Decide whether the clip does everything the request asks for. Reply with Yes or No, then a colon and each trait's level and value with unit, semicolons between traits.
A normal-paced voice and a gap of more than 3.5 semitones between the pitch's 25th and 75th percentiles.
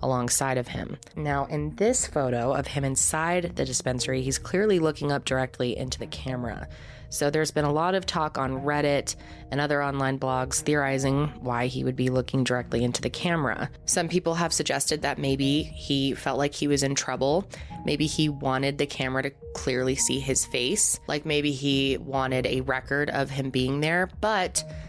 No: average, 185 wpm; narrow, 2.5 semitones